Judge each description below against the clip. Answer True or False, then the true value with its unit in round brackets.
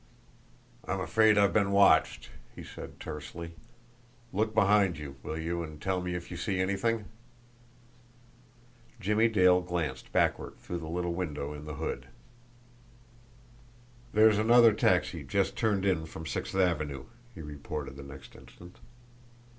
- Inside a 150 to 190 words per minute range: False (140 wpm)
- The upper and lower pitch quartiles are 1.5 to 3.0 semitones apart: False (4.2 semitones)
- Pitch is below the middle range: True (90 Hz)